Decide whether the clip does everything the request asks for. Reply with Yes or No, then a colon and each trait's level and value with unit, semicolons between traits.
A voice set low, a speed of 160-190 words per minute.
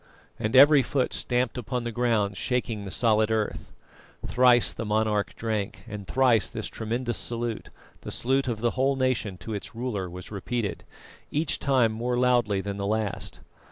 Yes: low, 115 Hz; average, 170 wpm